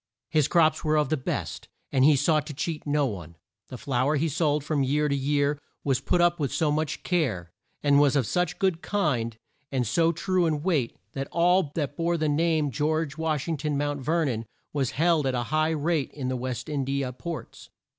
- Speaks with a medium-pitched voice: Yes, medium, 150 Hz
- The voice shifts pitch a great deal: No, average, 3.0 semitones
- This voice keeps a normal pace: No, fast, 225 wpm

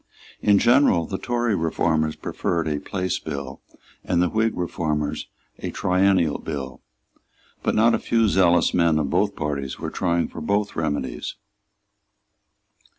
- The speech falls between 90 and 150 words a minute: Yes, average, 140 wpm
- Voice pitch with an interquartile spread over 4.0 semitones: Yes, average, 4.4 semitones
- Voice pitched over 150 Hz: No, very low, 85 Hz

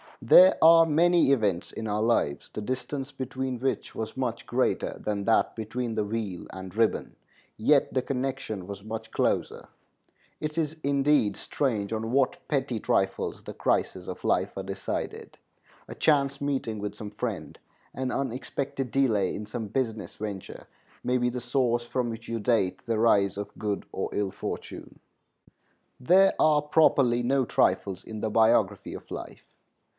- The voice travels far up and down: No, average, 4.2 semitones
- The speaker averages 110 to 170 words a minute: Yes, average, 160 wpm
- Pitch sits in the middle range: No, low, 120 Hz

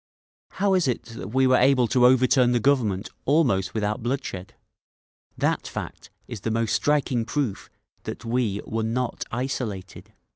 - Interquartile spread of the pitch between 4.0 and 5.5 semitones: No, average, 3.1 semitones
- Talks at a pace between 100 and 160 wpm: Yes, average, 150 wpm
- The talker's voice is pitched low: Yes, low, 120 Hz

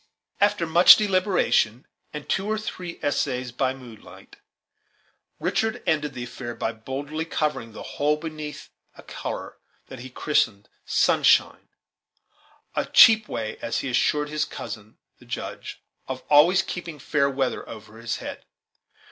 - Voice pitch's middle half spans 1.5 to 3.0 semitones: No, average, 5.0 semitones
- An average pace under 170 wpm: Yes, average, 140 wpm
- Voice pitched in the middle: Yes, medium, 145 Hz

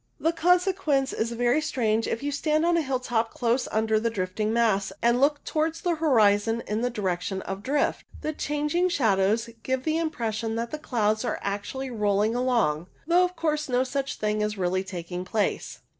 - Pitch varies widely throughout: Yes, wide, 5.7 semitones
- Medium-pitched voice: No, high, 235 Hz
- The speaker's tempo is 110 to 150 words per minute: No, average, 185 wpm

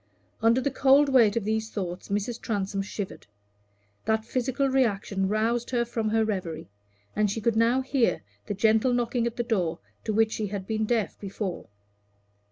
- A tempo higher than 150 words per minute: Yes, average, 175 wpm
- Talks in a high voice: Yes, high, 220 Hz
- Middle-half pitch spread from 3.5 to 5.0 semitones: No, average, 2.8 semitones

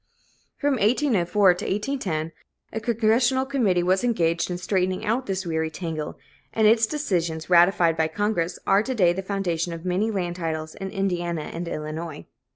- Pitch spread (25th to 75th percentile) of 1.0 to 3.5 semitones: No, average, 4.4 semitones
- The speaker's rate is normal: Yes, average, 165 wpm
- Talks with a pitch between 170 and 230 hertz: Yes, medium, 185 Hz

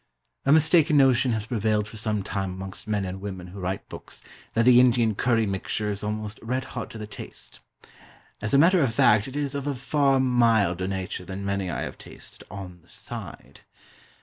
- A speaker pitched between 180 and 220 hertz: No, low, 110 Hz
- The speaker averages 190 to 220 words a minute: Yes, average, 200 wpm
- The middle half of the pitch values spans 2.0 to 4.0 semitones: No, average, 4.5 semitones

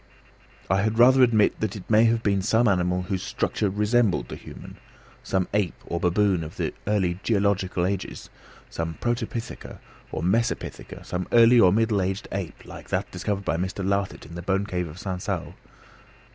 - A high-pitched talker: No, low, 100 Hz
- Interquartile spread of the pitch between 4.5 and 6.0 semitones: No, average, 3.3 semitones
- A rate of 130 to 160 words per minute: No, average, 175 wpm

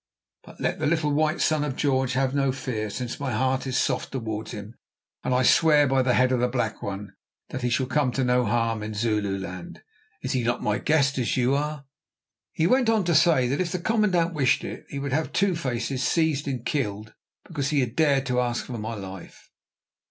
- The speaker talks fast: Yes, fast, 220 wpm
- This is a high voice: No, low, 130 Hz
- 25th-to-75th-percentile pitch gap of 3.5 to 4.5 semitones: Yes, average, 3.8 semitones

